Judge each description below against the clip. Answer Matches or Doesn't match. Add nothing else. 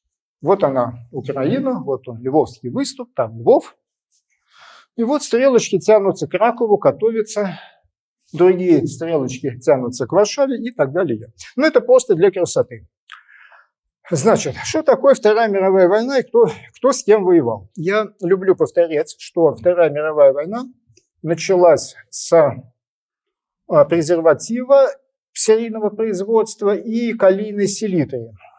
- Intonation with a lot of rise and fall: Matches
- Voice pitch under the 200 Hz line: Doesn't match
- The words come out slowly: Doesn't match